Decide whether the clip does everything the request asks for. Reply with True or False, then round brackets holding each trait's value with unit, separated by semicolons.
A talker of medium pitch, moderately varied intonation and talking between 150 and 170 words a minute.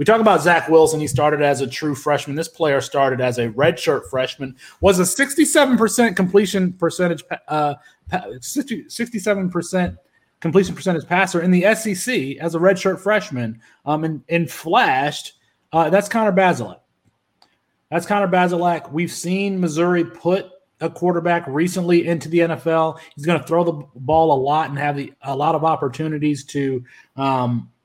True (170 Hz; 3.9 semitones; 160 wpm)